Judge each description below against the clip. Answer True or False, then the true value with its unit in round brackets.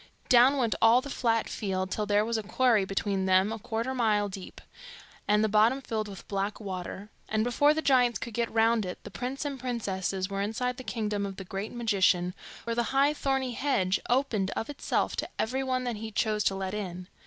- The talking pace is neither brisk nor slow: False (215 wpm)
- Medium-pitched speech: False (220 Hz)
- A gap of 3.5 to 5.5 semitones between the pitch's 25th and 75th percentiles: True (3.9 semitones)